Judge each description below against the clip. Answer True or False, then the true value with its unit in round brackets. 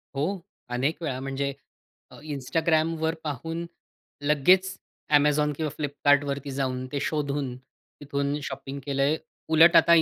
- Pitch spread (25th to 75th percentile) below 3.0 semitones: True (2.6 semitones)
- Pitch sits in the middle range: True (145 Hz)